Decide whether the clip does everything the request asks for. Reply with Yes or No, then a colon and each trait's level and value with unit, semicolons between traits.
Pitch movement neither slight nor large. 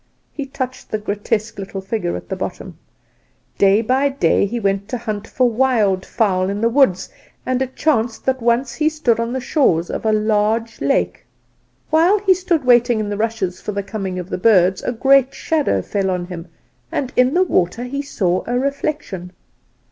Yes: average, 4.9 semitones